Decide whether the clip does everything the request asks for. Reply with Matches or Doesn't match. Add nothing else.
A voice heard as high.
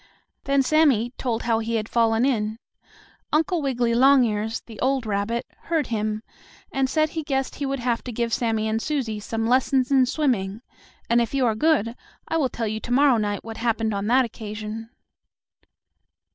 Matches